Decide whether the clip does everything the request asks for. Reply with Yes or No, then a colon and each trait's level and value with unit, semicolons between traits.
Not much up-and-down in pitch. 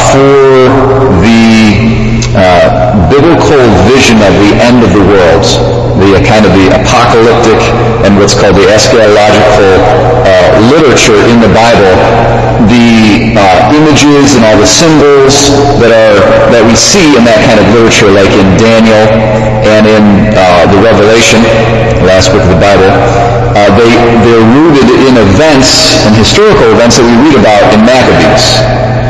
Yes: narrow, 2.3 semitones